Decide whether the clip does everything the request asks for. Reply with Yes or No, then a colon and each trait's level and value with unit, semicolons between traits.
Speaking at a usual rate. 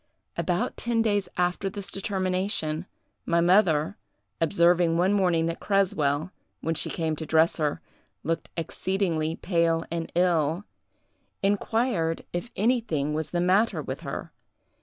No: slow, 130 wpm